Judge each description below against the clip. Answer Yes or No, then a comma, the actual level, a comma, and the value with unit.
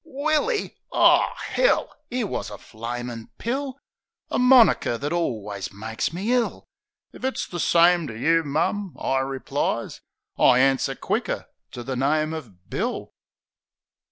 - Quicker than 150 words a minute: No, slow, 135 wpm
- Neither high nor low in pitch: Yes, medium, 155 Hz